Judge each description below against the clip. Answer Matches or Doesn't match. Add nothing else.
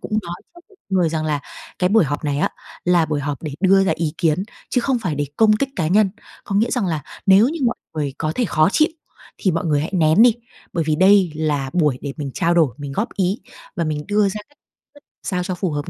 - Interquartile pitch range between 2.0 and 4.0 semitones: Doesn't match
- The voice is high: Doesn't match